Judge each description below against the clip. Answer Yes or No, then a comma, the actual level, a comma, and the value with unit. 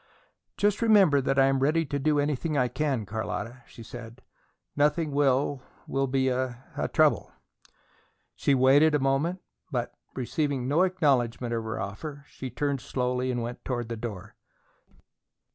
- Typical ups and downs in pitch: Yes, average, 3.1 semitones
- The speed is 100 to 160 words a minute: Yes, average, 150 wpm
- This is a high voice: No, low, 135 Hz